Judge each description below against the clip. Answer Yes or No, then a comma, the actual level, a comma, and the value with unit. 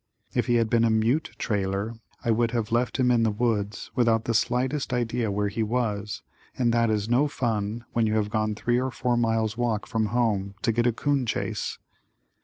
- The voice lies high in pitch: No, low, 115 Hz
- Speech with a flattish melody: Yes, narrow, 2.1 semitones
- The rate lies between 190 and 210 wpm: Yes, fast, 205 wpm